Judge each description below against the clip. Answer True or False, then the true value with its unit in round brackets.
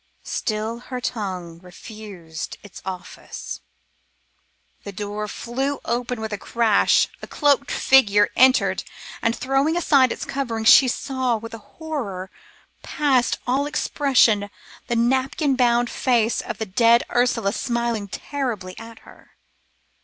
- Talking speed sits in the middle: False (125 wpm)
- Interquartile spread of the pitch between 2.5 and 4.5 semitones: True (3.9 semitones)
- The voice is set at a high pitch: True (235 Hz)